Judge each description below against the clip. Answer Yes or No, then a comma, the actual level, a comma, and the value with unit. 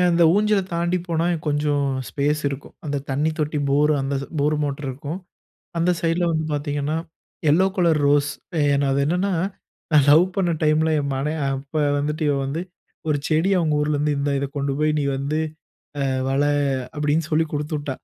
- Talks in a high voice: No, medium, 150 Hz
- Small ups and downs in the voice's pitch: Yes, narrow, 2.1 semitones